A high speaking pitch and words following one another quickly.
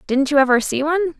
Yes: very high, 295 Hz; fast, 250 wpm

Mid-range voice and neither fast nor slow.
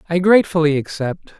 No: medium, 165 Hz; slow, 130 wpm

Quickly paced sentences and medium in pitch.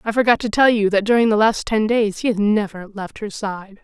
No: fast, 265 wpm; high, 210 Hz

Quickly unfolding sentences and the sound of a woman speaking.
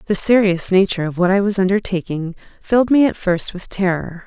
No: average, 195 wpm; female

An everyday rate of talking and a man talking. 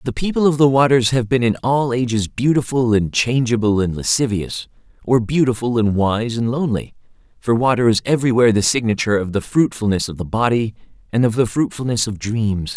Yes: average, 185 wpm; male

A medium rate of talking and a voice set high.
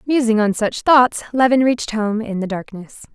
Yes: average, 190 wpm; high, 230 Hz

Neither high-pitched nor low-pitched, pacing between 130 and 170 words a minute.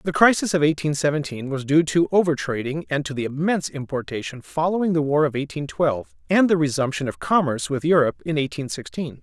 No: medium, 145 Hz; average, 200 wpm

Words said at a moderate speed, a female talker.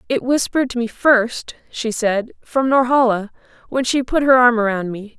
Yes: average, 175 wpm; female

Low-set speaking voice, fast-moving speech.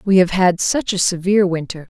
No: medium, 185 Hz; fast, 210 wpm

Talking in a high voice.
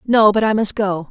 Yes: high, 205 Hz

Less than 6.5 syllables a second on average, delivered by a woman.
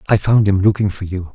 No: 6.1 syllables/s; male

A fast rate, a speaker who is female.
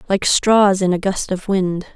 Yes: fast, 215 wpm; female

